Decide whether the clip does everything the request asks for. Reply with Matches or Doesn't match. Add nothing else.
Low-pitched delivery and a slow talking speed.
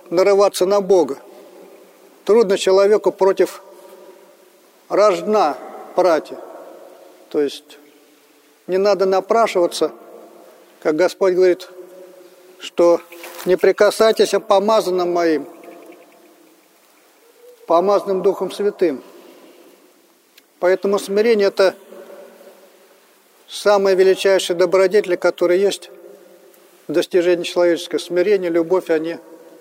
Doesn't match